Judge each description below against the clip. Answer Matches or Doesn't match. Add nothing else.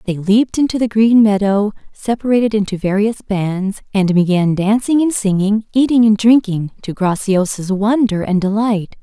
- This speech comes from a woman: Matches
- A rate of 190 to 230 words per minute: Doesn't match